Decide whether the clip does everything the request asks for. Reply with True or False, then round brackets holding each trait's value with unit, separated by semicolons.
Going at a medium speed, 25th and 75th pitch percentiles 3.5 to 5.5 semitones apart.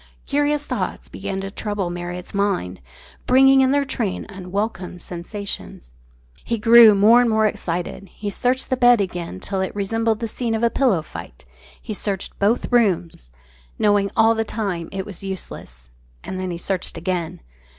True (165 wpm; 4.1 semitones)